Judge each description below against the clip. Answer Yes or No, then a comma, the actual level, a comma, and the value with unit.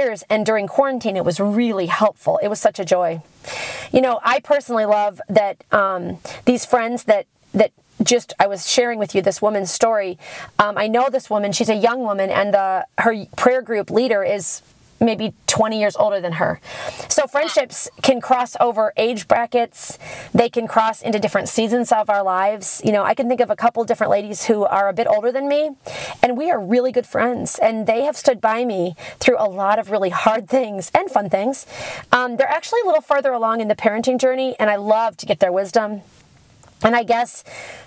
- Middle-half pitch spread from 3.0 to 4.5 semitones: Yes, average, 3.5 semitones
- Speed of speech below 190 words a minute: No, fast, 205 wpm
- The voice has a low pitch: No, high, 220 Hz